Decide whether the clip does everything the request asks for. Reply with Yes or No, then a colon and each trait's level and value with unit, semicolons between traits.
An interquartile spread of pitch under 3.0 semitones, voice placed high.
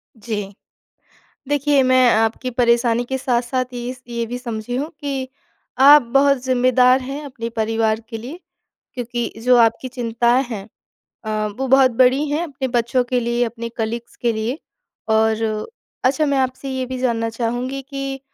Yes: narrow, 2.4 semitones; very high, 250 Hz